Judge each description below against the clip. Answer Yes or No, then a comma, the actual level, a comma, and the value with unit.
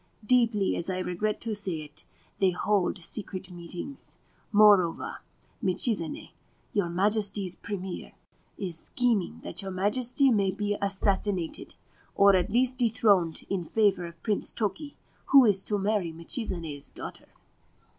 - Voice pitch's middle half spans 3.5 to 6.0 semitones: No, average, 3.0 semitones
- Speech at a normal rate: No, slow, 130 wpm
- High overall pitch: Yes, high, 200 Hz